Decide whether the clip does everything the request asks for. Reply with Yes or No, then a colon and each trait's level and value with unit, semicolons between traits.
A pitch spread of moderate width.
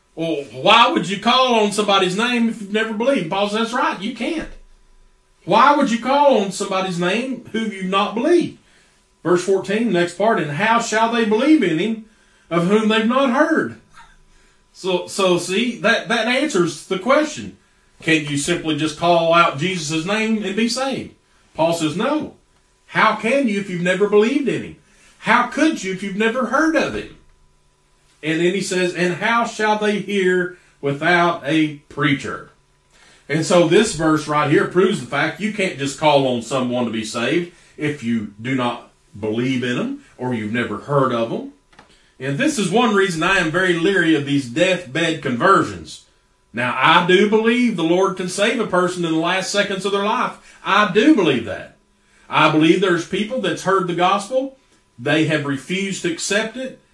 No: wide, 5.7 semitones